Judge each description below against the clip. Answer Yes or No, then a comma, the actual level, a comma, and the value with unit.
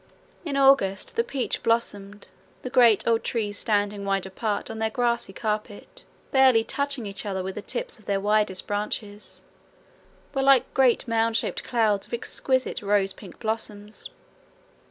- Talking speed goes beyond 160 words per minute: No, average, 155 wpm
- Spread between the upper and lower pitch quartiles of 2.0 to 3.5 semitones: Yes, average, 3.1 semitones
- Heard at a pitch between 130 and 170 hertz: No, high, 220 Hz